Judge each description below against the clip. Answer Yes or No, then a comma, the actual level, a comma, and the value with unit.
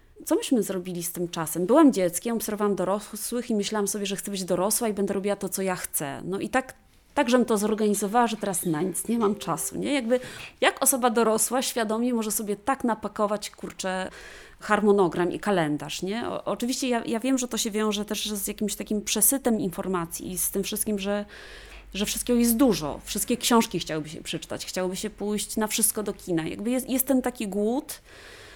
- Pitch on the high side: Yes, high, 210 Hz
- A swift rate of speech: Yes, fast, 200 wpm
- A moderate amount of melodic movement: Yes, average, 3.6 semitones